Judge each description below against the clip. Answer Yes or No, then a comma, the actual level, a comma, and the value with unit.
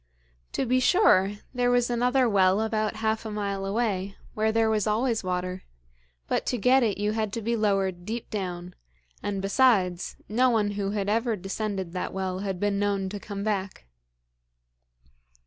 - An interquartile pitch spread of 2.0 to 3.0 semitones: Yes, average, 2.7 semitones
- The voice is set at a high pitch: Yes, high, 205 Hz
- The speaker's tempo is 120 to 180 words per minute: Yes, average, 170 wpm